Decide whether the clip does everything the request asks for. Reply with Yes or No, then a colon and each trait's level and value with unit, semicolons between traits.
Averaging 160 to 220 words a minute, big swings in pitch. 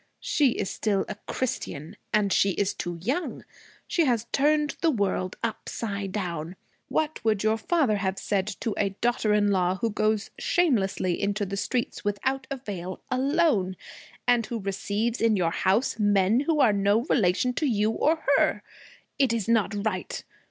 No: average, 165 wpm; average, 4.2 semitones